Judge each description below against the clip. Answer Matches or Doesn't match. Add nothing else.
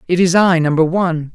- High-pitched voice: Doesn't match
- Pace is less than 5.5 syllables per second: Doesn't match